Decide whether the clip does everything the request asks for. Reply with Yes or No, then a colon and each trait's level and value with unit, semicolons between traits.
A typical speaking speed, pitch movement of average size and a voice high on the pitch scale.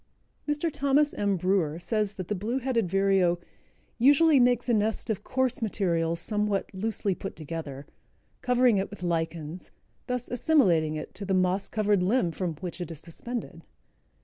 No: average, 160 wpm; wide, 5.8 semitones; high, 200 Hz